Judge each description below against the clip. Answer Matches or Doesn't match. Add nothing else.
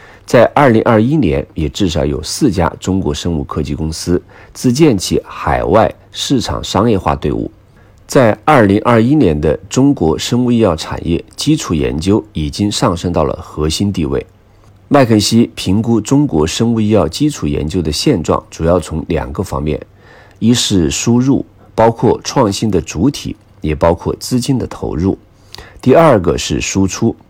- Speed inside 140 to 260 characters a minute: Matches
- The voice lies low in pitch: Matches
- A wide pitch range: Matches